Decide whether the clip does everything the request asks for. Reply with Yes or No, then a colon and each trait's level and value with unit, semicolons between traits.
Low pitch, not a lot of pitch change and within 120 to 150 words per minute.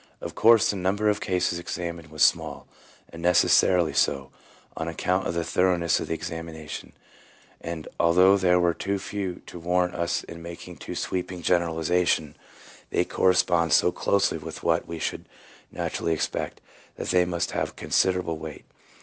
No: very low, 85 Hz; narrow, 1.8 semitones; average, 165 wpm